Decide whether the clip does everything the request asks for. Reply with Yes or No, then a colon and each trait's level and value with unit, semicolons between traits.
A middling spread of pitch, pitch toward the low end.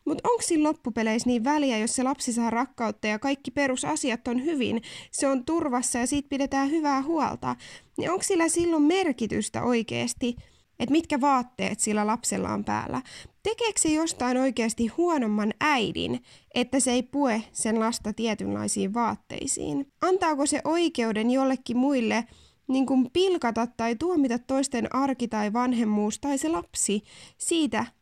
No: average, 4.5 semitones; very high, 260 Hz